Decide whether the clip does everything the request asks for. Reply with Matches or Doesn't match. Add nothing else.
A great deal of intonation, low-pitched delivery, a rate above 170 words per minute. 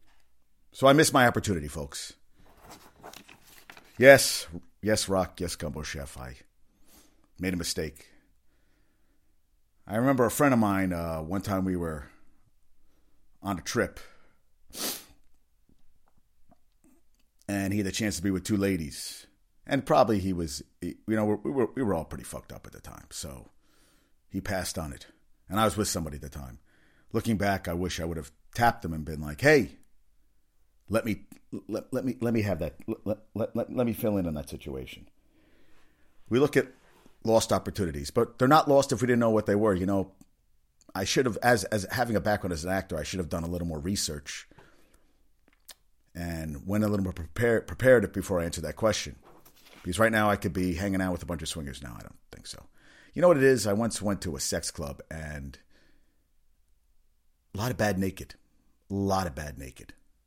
Matches